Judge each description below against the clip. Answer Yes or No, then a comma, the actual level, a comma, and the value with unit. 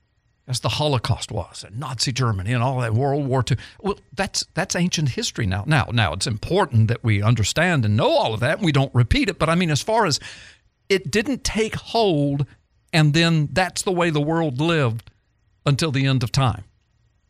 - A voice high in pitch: No, low, 135 Hz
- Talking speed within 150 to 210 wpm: Yes, fast, 205 wpm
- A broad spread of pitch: Yes, wide, 6.5 semitones